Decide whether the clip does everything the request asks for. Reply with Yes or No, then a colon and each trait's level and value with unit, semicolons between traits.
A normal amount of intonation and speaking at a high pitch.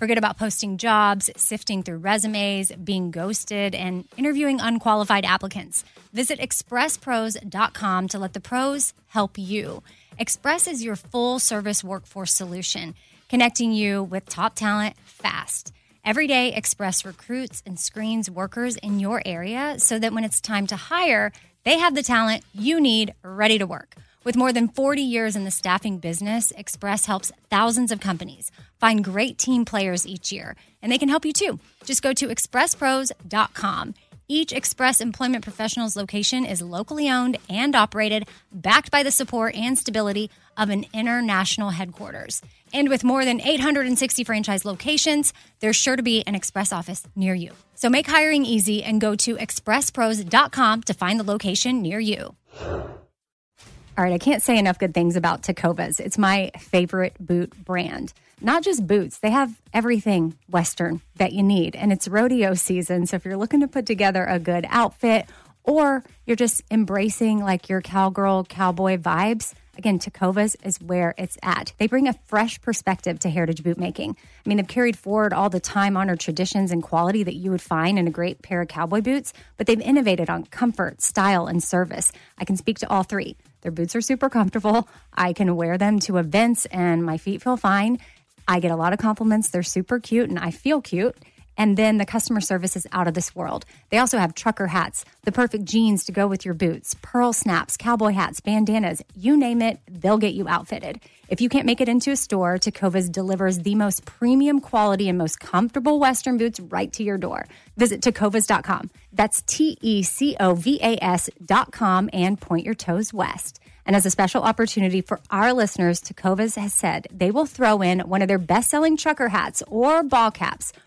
Yes: average, 4.0 semitones; high, 210 Hz